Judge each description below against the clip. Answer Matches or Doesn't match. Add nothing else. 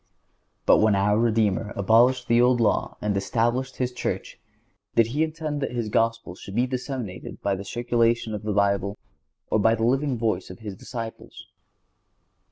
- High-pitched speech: Doesn't match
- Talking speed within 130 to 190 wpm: Matches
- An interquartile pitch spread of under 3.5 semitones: Matches